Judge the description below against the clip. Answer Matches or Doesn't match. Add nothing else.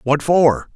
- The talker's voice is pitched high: Doesn't match